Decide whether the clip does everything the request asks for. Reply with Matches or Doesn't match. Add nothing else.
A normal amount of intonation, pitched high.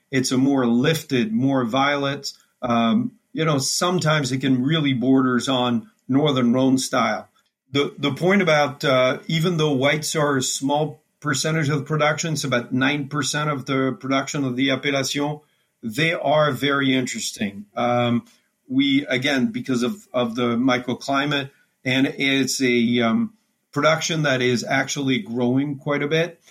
Doesn't match